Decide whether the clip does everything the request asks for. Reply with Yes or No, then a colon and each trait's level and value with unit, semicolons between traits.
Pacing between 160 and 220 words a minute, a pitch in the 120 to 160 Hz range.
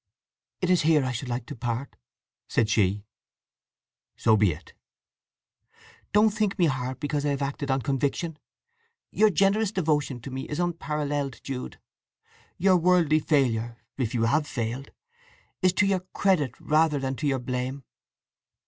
No: average, 150 wpm; medium, 140 Hz